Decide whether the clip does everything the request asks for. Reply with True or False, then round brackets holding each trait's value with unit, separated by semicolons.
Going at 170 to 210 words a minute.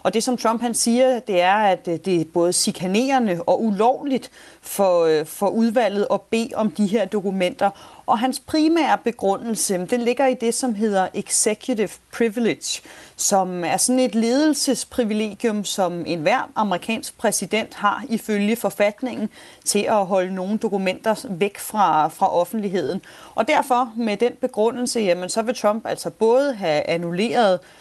False (150 wpm)